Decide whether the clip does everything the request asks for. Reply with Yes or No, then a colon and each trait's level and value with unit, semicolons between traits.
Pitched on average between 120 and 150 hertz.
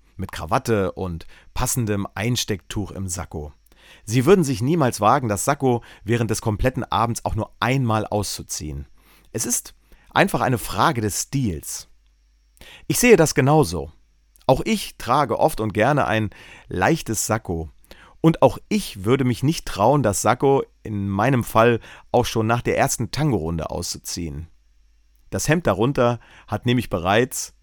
No: low, 110 Hz